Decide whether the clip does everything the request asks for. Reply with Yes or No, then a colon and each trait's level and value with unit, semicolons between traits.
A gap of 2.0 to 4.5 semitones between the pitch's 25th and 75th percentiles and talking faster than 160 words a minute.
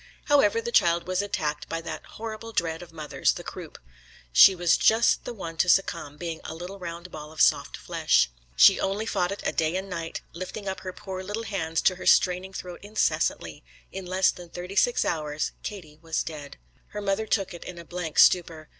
Yes: average, 3.2 semitones; fast, 205 wpm